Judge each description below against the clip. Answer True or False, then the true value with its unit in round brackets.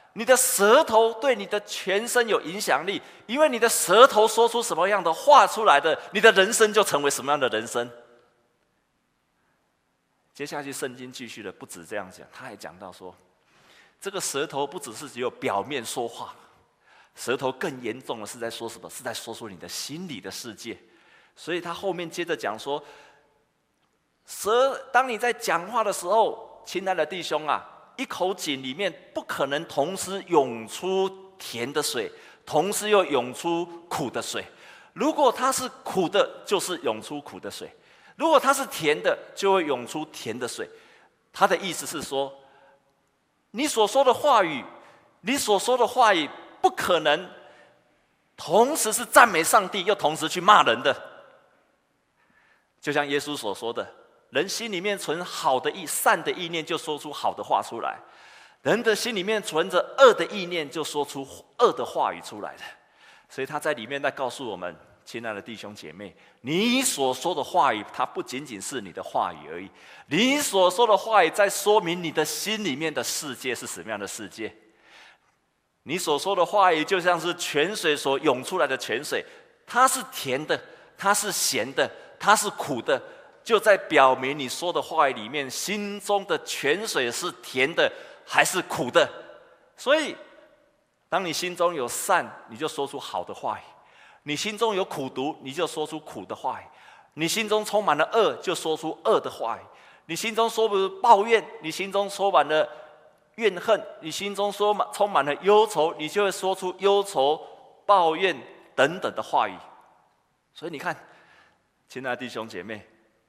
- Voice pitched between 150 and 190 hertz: True (185 Hz)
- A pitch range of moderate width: False (7.4 semitones)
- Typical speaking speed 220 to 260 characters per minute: True (245 characters per minute)